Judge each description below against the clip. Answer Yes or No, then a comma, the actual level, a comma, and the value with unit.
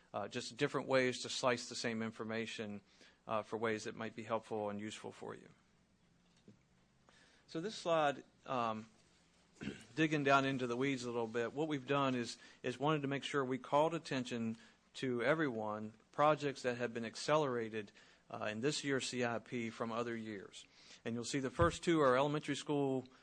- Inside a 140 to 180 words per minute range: Yes, average, 175 wpm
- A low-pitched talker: Yes, low, 125 Hz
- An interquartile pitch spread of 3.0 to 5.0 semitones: Yes, average, 3.8 semitones